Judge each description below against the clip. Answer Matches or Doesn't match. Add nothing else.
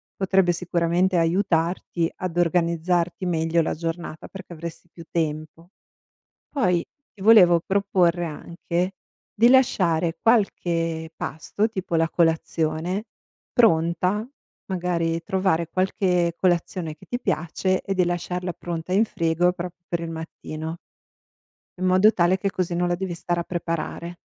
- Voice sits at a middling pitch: Matches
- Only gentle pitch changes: Matches